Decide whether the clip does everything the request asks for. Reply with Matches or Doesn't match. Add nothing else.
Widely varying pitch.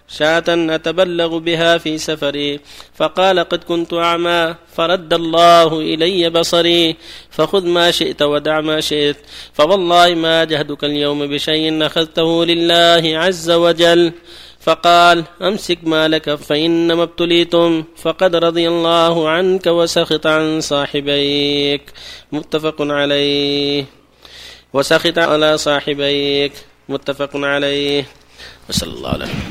Doesn't match